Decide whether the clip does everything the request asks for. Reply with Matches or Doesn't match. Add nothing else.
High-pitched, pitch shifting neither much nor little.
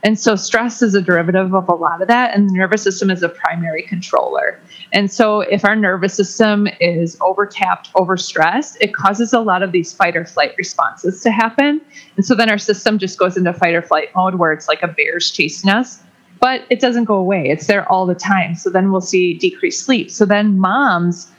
Matches